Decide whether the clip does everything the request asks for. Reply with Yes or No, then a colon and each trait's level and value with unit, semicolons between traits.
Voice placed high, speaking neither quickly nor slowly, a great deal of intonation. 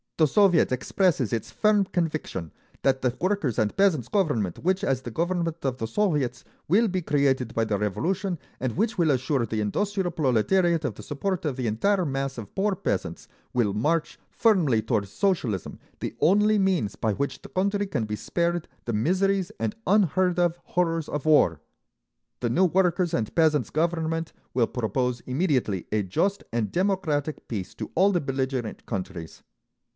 No: medium, 150 Hz; average, 170 wpm; wide, 7.8 semitones